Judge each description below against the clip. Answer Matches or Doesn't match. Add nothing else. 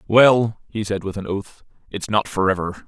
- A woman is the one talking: Doesn't match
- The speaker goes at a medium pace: Matches